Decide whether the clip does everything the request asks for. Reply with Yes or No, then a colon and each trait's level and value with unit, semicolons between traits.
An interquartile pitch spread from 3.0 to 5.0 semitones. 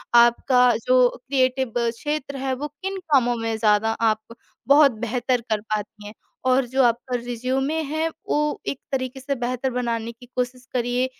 No: narrow, 2.4 semitones